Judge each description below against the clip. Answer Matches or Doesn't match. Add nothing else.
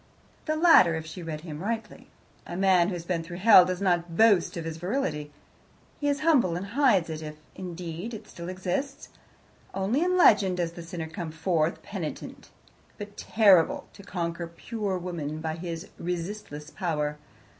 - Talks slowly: Doesn't match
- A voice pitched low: Doesn't match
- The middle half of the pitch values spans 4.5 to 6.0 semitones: Doesn't match